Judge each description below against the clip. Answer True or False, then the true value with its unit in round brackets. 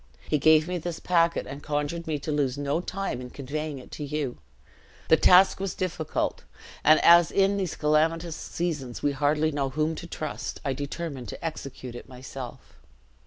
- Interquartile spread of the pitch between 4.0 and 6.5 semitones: False (3.2 semitones)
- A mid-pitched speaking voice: True (155 Hz)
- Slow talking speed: False (175 wpm)